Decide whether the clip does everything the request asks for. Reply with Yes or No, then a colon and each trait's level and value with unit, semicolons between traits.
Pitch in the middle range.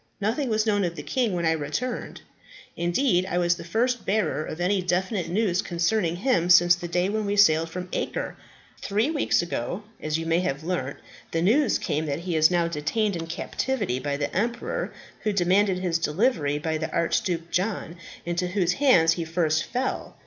Yes: medium, 175 Hz